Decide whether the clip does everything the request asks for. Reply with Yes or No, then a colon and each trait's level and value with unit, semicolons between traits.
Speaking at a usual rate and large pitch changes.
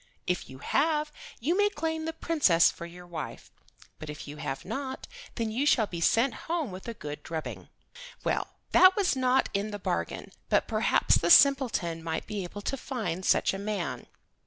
Yes: average, 185 wpm; wide, 8.7 semitones